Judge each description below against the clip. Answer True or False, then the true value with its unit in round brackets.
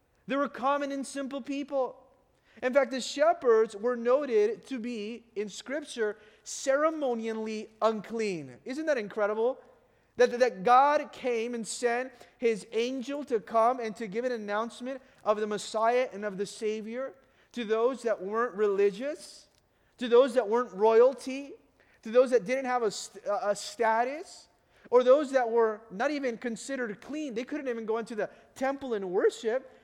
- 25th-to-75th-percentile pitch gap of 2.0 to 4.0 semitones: True (3.3 semitones)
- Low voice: False (240 Hz)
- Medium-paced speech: True (155 wpm)